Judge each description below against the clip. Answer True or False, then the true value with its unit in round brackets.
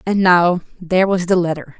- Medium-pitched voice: True (175 Hz)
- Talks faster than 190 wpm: False (165 wpm)